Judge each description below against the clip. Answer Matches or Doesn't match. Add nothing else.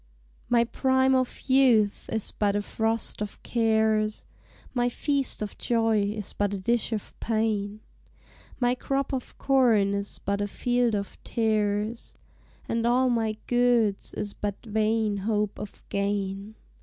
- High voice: Matches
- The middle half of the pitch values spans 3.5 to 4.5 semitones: Doesn't match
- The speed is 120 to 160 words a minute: Matches